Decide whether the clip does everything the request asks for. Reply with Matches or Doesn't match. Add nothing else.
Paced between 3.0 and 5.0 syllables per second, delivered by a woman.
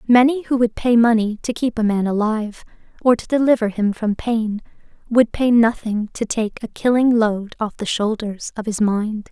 Matches